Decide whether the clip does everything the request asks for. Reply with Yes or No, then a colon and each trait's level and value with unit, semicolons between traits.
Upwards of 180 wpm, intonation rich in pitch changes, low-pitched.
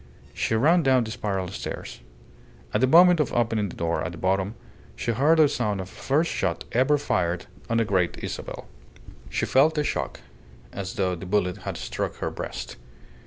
Yes: average, 190 wpm; wide, 6.4 semitones; low, 110 Hz